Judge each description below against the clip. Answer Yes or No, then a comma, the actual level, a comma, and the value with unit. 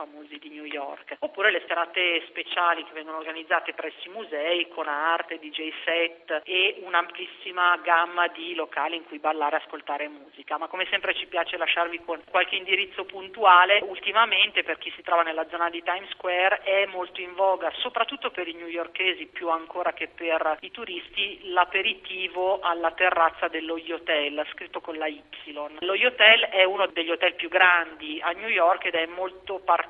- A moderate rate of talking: No, fast, 175 wpm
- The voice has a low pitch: No, medium, 170 Hz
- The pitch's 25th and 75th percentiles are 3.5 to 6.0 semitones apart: No, narrow, 2.5 semitones